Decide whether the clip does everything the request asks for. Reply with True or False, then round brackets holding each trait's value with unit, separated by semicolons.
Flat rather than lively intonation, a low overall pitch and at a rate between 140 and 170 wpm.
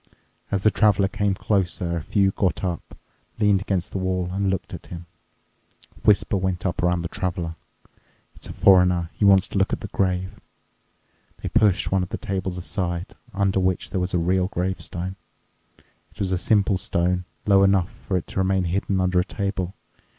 False (1.5 semitones; 95 Hz; 185 wpm)